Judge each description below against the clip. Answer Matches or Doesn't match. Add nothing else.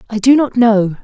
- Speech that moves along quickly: Matches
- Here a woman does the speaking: Matches